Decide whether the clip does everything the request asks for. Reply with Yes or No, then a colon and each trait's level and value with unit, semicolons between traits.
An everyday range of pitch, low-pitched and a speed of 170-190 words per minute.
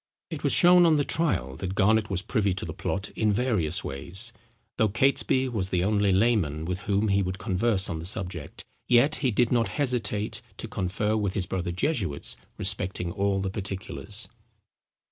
Yes: average, 3.9 semitones; low, 100 Hz; average, 180 wpm